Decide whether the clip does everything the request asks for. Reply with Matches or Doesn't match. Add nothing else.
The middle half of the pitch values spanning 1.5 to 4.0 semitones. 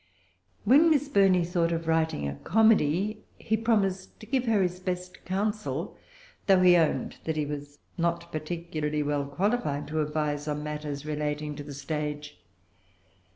Doesn't match